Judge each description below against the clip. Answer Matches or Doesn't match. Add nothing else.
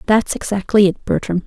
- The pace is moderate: Matches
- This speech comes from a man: Doesn't match